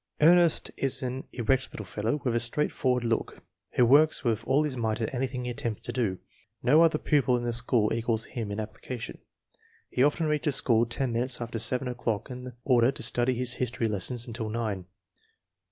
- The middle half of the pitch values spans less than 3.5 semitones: Yes, narrow, 2.5 semitones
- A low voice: Yes, low, 125 Hz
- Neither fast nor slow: Yes, average, 190 wpm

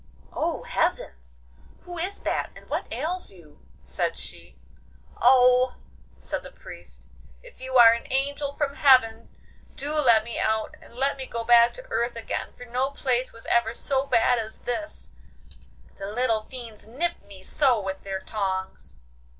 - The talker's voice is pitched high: Yes, high, 240 Hz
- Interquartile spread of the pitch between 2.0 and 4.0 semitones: Yes, average, 3.7 semitones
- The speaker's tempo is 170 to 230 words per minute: No, average, 160 wpm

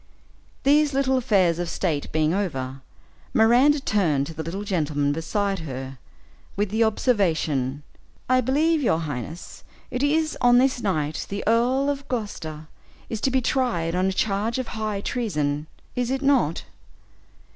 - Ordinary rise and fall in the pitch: No, wide, 8.2 semitones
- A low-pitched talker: No, high, 205 Hz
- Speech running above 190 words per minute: No, average, 150 wpm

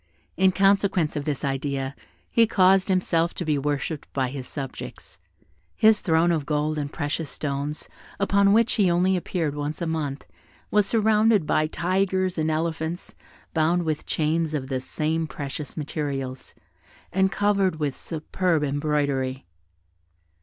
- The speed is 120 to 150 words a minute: Yes, average, 140 wpm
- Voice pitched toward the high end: No, medium, 160 Hz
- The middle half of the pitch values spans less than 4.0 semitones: No, average, 4.3 semitones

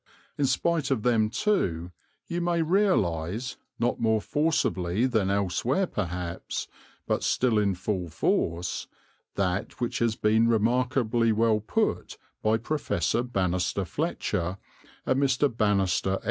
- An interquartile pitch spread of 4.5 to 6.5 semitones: Yes, average, 5.2 semitones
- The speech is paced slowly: Yes, slow, 125 wpm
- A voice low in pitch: Yes, low, 110 Hz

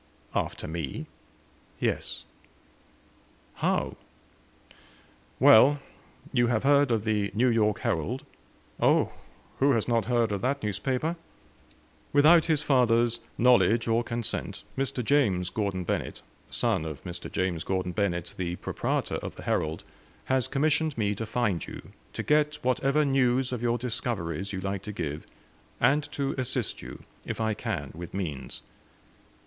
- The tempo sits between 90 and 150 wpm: Yes, average, 140 wpm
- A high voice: No, low, 115 Hz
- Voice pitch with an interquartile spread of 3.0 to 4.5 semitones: No, wide, 5.4 semitones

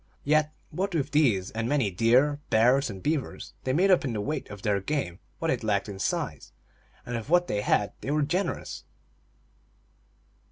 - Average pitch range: No, wide, 6.4 semitones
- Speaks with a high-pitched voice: No, low, 130 Hz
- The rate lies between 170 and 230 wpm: Yes, average, 185 wpm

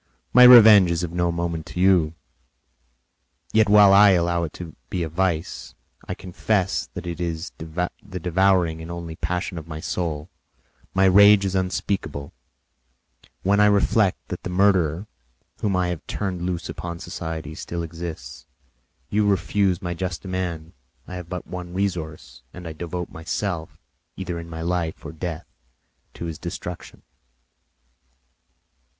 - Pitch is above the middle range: No, very low, 90 Hz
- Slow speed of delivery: No, average, 150 wpm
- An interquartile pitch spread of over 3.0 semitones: No, narrow, 2.4 semitones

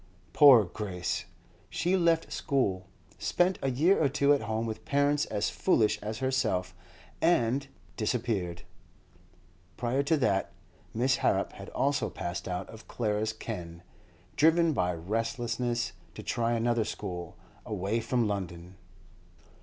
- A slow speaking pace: Yes, slow, 125 wpm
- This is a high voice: No, low, 115 Hz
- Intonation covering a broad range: Yes, wide, 5.8 semitones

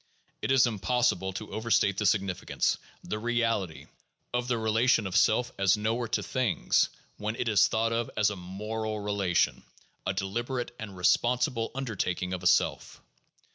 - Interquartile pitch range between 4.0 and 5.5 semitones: No, average, 3.4 semitones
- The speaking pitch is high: No, low, 110 Hz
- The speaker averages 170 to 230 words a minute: No, average, 155 wpm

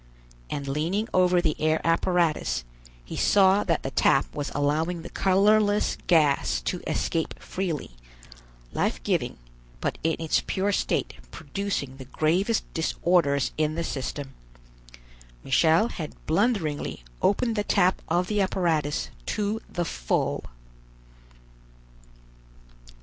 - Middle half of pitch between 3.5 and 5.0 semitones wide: Yes, average, 4.5 semitones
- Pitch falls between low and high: Yes, medium, 165 Hz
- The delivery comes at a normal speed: No, slow, 115 wpm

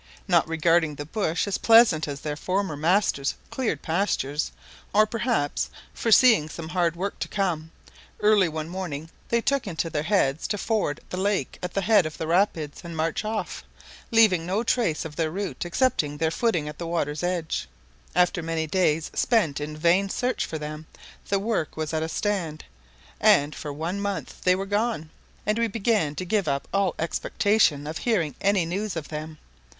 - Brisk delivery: No, average, 180 wpm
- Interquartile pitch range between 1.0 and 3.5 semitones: No, average, 4.6 semitones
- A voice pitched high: No, medium, 175 Hz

